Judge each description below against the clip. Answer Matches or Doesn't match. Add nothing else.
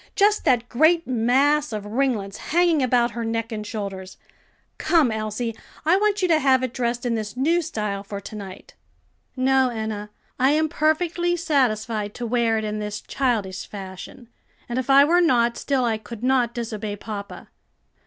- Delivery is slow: Doesn't match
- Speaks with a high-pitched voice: Matches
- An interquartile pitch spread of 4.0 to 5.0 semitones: Matches